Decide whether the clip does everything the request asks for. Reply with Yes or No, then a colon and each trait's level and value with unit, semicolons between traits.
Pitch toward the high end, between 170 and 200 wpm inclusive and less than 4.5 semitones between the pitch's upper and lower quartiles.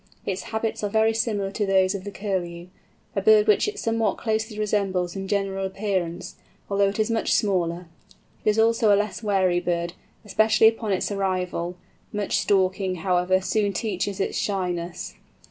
No: high, 195 Hz; average, 160 wpm; average, 2.7 semitones